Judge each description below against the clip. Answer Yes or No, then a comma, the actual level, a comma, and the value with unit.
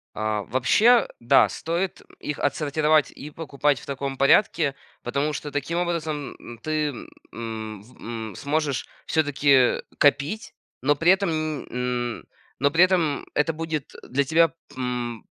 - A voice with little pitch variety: No, average, 3.2 semitones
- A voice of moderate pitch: Yes, medium, 145 Hz